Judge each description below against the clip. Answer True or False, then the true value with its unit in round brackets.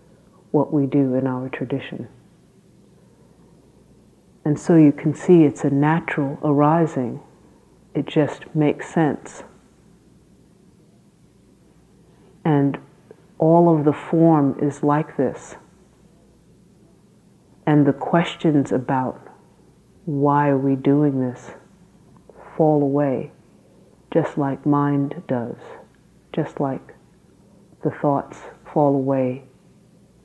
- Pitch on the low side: False (145 Hz)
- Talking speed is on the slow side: True (95 wpm)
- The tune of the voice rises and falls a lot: False (2.3 semitones)